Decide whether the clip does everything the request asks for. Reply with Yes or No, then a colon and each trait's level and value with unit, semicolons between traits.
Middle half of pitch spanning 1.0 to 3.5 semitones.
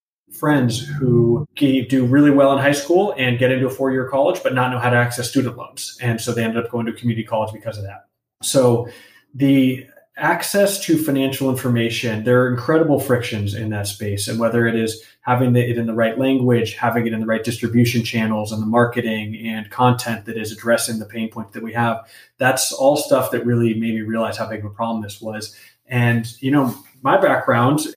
Yes: narrow, 2.4 semitones